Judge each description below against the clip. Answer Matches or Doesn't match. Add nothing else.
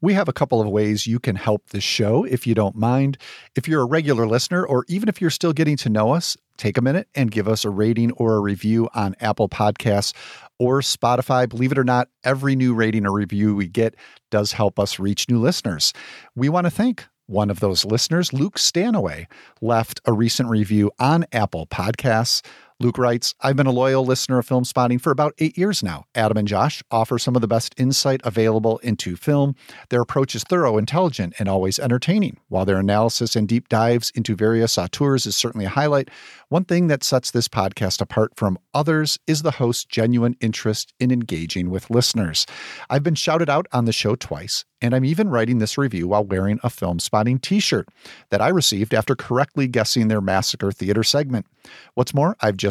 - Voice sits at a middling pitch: Doesn't match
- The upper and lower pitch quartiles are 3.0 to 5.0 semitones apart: Matches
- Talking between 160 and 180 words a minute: Doesn't match